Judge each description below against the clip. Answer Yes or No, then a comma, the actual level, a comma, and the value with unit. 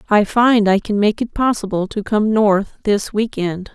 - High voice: Yes, high, 210 Hz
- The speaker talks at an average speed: No, fast, 210 wpm